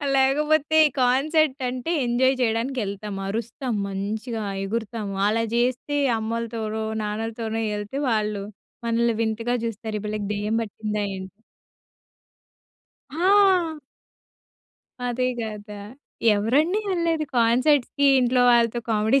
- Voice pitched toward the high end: Yes, high, 230 Hz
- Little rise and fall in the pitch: No, average, 3.8 semitones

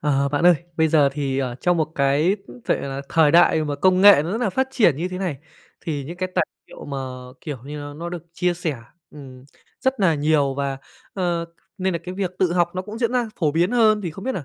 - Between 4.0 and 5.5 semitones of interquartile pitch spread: Yes, average, 4.3 semitones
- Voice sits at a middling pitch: Yes, medium, 165 Hz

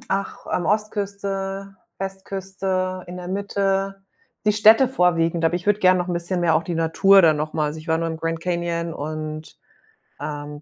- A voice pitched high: No, medium, 180 Hz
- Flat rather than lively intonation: No, average, 3.0 semitones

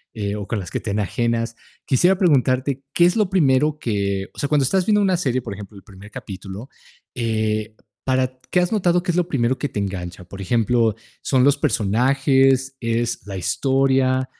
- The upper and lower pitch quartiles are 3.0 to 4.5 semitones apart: No, average, 5.2 semitones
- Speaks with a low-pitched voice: Yes, low, 125 Hz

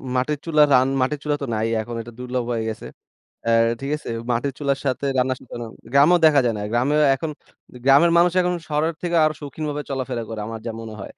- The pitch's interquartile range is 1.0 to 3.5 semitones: No, average, 3.9 semitones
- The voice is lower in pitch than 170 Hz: Yes, low, 135 Hz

